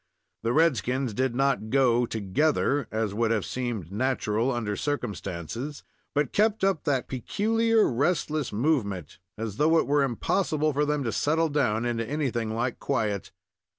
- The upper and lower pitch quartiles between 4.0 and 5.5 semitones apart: Yes, average, 4.9 semitones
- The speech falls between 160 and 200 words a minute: No, average, 150 wpm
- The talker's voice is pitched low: Yes, low, 130 Hz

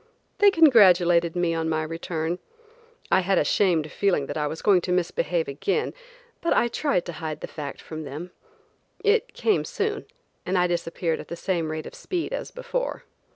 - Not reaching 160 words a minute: No, average, 185 wpm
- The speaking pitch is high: No, medium, 175 Hz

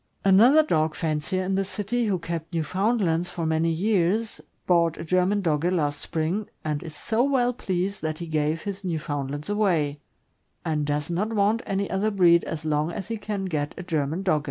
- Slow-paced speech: No, average, 190 wpm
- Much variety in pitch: No, average, 4.2 semitones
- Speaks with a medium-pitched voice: Yes, medium, 175 Hz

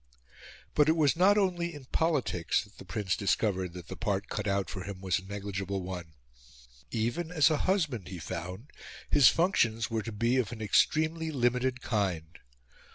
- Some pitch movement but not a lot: No, wide, 7.8 semitones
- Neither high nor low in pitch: No, low, 110 Hz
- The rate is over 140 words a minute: Yes, average, 175 wpm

